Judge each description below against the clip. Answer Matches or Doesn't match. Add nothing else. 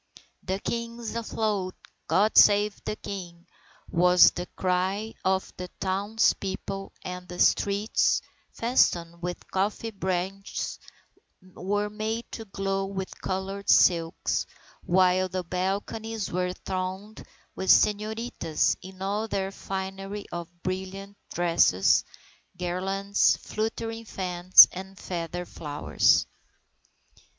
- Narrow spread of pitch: Matches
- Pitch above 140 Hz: Matches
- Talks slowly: Matches